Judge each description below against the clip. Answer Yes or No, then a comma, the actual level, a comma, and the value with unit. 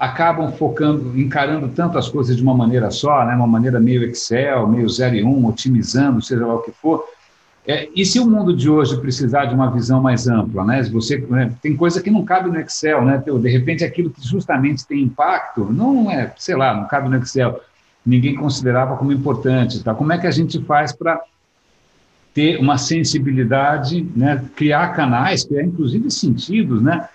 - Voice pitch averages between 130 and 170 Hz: Yes, low, 135 Hz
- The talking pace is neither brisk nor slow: Yes, average, 190 wpm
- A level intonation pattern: No, average, 3.7 semitones